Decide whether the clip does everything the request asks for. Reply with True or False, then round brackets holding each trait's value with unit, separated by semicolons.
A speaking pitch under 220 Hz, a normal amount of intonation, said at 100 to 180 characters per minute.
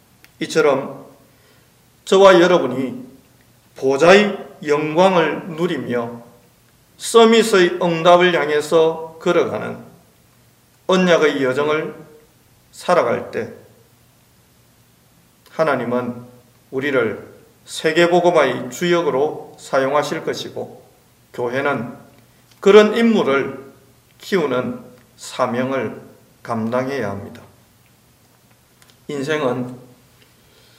False (135 Hz; 5.8 semitones; 175 characters per minute)